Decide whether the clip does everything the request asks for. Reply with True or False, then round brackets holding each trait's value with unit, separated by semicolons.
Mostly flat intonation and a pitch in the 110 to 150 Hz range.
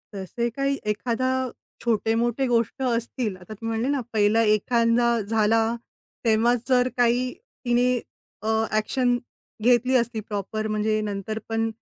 False (2.1 semitones; 230 Hz)